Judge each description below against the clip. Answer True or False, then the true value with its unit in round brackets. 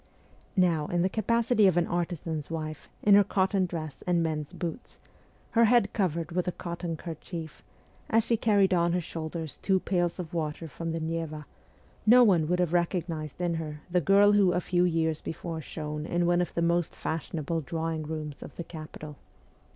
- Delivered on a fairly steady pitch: True (2.3 semitones)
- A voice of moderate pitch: True (170 Hz)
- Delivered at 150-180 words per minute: False (190 wpm)